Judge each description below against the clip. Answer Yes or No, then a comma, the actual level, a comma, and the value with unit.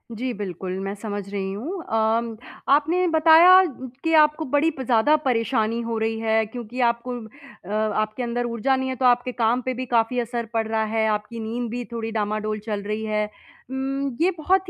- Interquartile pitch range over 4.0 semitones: No, average, 3.2 semitones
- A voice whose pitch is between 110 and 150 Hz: No, high, 235 Hz